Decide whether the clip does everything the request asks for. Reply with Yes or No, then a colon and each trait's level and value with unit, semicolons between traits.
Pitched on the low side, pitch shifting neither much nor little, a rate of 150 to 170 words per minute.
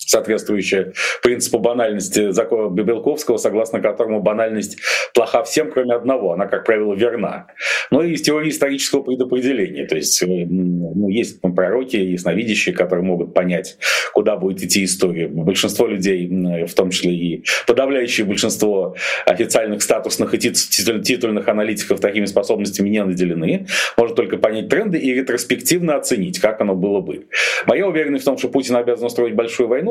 No: low, 110 Hz; wide, 5.8 semitones; average, 155 wpm